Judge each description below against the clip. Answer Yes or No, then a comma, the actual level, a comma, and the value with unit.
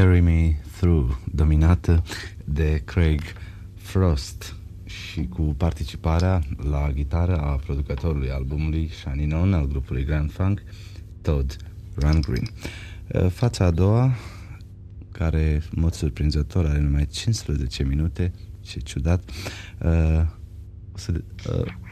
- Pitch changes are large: No, average, 3.6 semitones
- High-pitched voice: No, very low, 85 Hz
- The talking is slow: Yes, slow, 110 wpm